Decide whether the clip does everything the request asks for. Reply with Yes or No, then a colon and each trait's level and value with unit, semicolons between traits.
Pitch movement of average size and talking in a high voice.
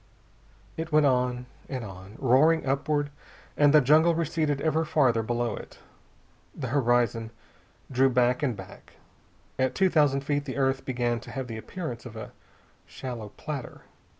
No: average, 3.7 semitones; low, 130 Hz